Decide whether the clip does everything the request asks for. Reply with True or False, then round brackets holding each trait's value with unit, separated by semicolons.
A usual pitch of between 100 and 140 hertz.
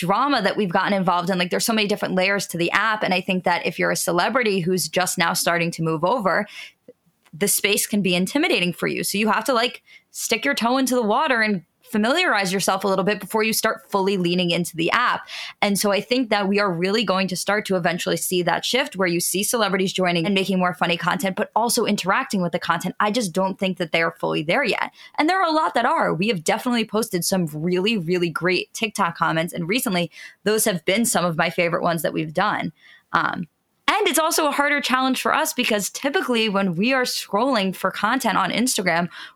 False (195 Hz)